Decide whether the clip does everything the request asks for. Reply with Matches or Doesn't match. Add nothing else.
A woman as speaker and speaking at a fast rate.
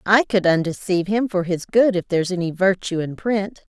Matches